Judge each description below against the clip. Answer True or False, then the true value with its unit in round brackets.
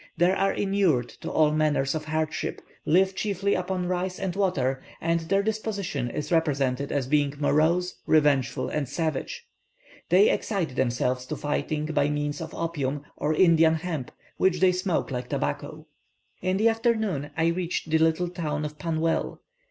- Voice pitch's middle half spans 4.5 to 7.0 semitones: False (3.8 semitones)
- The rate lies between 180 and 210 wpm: False (160 wpm)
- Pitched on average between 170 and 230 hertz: False (160 Hz)